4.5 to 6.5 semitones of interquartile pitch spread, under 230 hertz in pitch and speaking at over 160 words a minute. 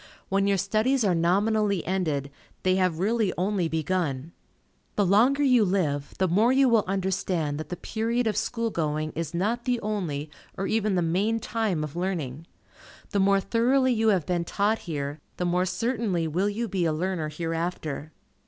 Yes: average, 4.8 semitones; high, 190 Hz; average, 175 wpm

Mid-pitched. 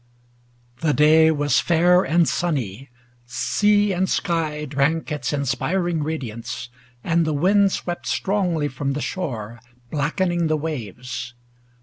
Yes: medium, 155 Hz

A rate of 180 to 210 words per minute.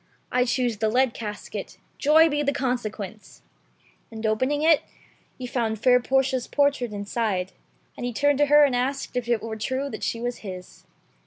Yes: average, 185 wpm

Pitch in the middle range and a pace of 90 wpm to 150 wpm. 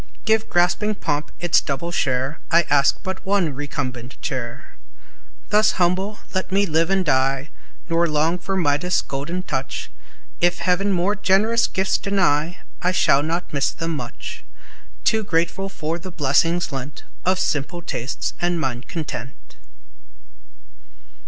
Yes: medium, 170 Hz; average, 140 wpm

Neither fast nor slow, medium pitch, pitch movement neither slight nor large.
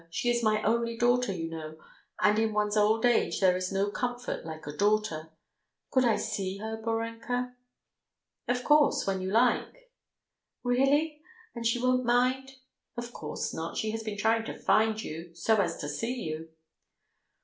No: average, 170 wpm; high, 220 Hz; average, 4.1 semitones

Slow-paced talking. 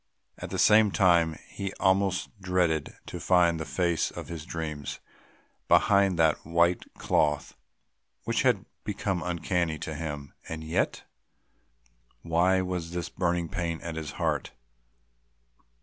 Yes: slow, 130 wpm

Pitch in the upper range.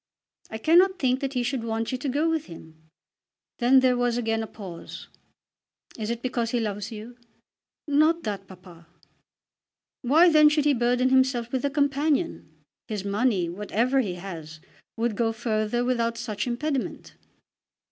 Yes: high, 240 Hz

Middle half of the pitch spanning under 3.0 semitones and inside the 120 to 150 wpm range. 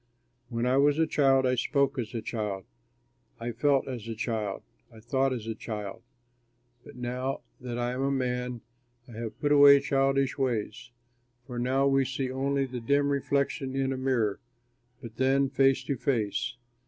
No: narrow, 2.5 semitones; average, 175 wpm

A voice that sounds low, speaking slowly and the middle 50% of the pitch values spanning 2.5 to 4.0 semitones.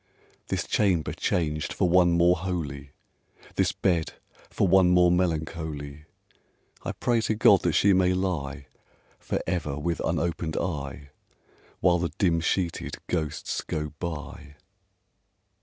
Yes: very low, 85 Hz; slow, 125 wpm; average, 3.0 semitones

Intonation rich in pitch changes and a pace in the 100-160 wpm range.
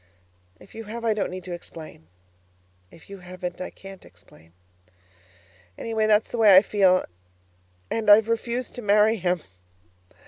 No: average, 3.3 semitones; average, 150 wpm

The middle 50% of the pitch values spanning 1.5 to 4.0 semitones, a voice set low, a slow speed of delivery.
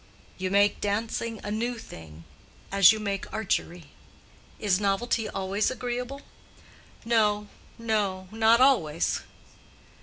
No: average, 2.9 semitones; high, 210 Hz; slow, 100 wpm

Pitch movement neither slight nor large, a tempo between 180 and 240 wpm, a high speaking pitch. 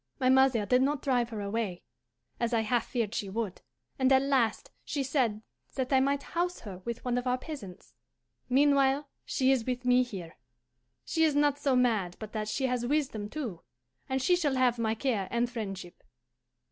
Yes: average, 3.6 semitones; average, 190 wpm; very high, 250 Hz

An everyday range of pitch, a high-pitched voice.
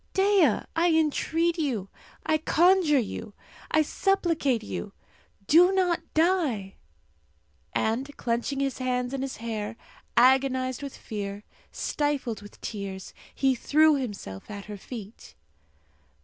No: wide, 6.3 semitones; very high, 265 Hz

